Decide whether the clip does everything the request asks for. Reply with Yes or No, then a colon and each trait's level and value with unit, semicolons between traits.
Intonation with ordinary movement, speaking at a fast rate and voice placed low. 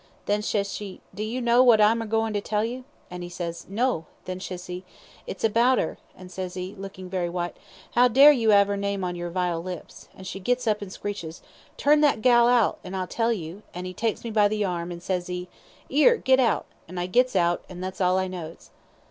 No: average, 4.0 semitones; fast, 235 wpm; high, 195 Hz